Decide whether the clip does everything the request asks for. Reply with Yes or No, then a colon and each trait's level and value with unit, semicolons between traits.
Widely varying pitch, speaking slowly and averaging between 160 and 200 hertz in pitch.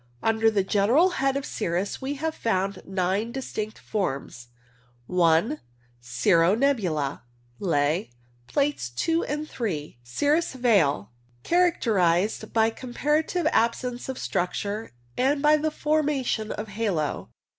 No: wide, 7.7 semitones; slow, 125 wpm; high, 220 Hz